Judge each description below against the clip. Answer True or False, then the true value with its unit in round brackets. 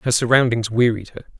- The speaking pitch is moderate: False (120 Hz)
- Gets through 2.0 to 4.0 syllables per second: False (5.4 syllables/s)